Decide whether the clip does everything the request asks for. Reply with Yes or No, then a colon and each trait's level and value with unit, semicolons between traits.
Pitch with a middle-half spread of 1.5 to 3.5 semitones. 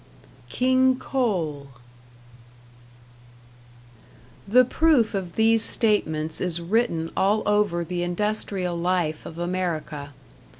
No: average, 4.8 semitones